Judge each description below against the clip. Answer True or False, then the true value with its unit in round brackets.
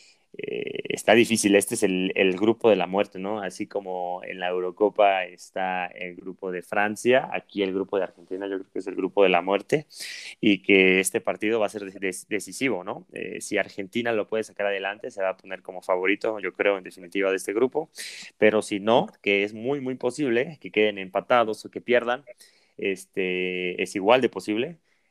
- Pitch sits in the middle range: False (100 Hz)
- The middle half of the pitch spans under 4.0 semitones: True (2.8 semitones)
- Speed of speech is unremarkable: False (205 wpm)